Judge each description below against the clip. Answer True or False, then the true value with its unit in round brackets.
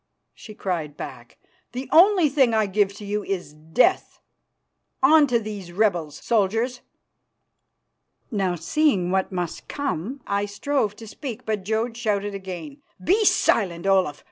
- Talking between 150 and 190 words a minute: False (140 wpm)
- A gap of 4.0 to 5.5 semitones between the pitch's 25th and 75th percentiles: True (5.1 semitones)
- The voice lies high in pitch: True (210 Hz)